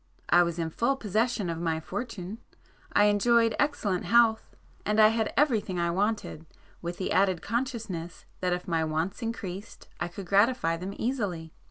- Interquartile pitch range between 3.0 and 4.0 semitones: No, average, 4.7 semitones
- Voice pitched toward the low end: No, high, 200 Hz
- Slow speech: No, average, 170 wpm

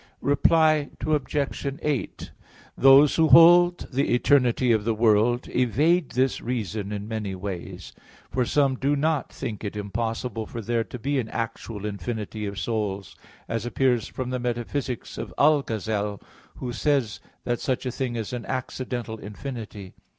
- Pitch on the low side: Yes, low, 120 Hz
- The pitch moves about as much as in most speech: Yes, average, 4.0 semitones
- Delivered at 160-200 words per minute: No, average, 150 wpm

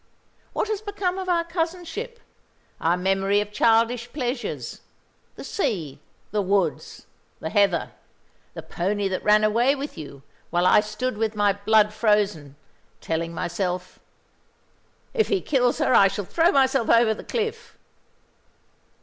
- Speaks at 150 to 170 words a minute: No, average, 140 wpm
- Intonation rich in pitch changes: Yes, wide, 6.8 semitones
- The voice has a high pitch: Yes, high, 215 Hz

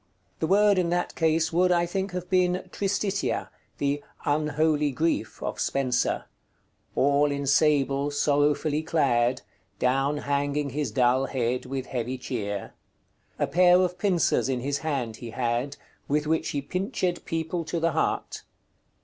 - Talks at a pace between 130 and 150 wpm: Yes, average, 145 wpm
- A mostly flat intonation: No, average, 4.1 semitones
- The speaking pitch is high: No, medium, 145 Hz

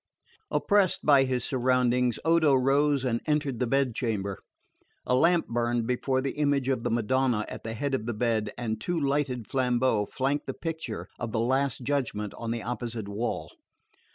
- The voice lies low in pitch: Yes, low, 125 Hz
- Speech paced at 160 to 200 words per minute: Yes, average, 175 wpm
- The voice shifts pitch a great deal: No, average, 3.1 semitones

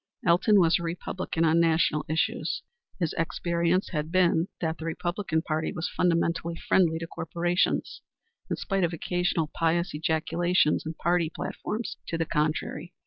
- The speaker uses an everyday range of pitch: No, narrow, 1.5 semitones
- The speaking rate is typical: Yes, average, 145 wpm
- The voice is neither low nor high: Yes, medium, 170 Hz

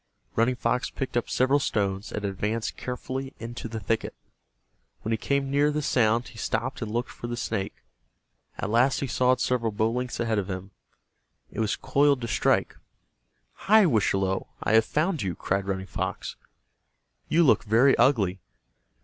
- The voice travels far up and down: No, average, 3.7 semitones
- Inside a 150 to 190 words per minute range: Yes, average, 170 wpm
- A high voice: No, low, 115 Hz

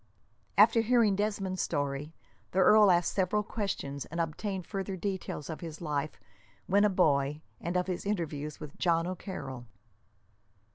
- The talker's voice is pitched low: No, medium, 180 Hz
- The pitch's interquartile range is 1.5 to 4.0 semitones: No, average, 4.6 semitones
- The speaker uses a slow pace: No, average, 145 wpm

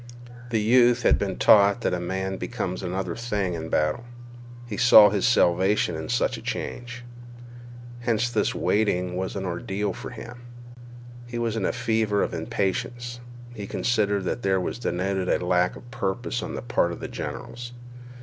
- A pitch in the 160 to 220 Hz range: No, low, 105 Hz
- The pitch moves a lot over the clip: No, average, 4.2 semitones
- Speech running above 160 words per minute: Yes, average, 170 wpm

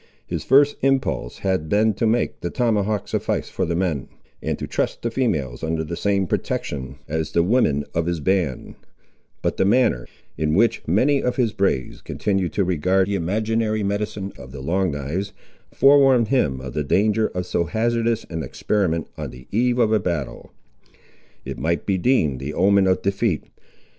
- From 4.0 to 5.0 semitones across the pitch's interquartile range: No, wide, 5.6 semitones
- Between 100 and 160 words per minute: No, average, 180 wpm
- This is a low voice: Yes, very low, 95 Hz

